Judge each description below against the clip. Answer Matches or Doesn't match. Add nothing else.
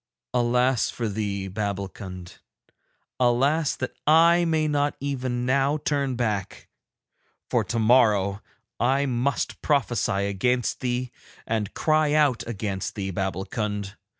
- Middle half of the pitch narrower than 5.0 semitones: Doesn't match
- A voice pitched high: Doesn't match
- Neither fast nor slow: Doesn't match